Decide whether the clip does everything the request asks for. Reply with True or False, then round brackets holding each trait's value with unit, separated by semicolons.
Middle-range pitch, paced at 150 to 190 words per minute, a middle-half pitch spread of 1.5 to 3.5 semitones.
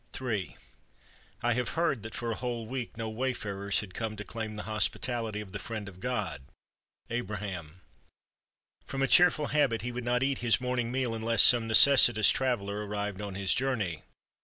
False (115 Hz; 175 wpm; 3.1 semitones)